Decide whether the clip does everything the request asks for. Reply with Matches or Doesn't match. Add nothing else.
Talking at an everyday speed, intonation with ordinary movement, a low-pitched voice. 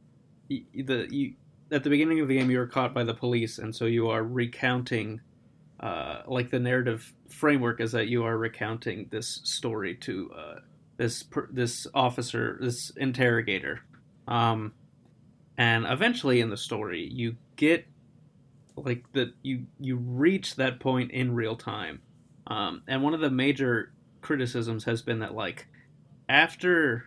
Matches